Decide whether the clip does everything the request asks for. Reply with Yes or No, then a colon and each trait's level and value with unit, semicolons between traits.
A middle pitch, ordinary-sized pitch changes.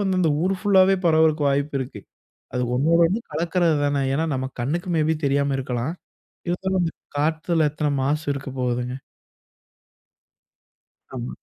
Yes: medium, 155 Hz; average, 3.8 semitones